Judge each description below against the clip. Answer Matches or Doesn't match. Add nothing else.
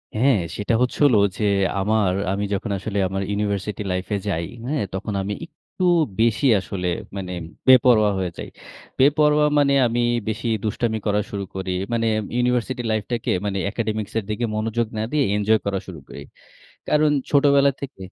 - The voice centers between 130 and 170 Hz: Doesn't match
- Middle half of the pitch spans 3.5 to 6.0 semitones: Matches